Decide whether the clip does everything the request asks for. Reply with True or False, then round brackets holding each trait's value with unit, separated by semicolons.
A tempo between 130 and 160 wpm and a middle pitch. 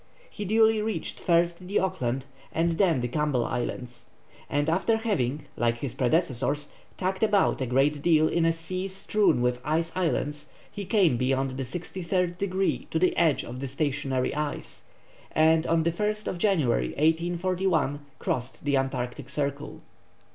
True (155 wpm; 160 Hz)